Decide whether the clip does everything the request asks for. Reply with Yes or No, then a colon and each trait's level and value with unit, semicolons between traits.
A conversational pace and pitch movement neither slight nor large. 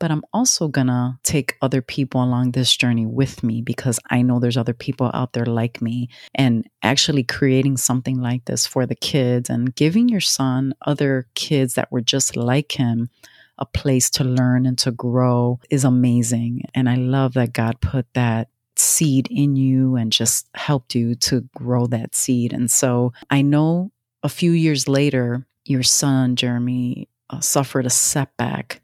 No: average, 175 wpm; narrow, 2.0 semitones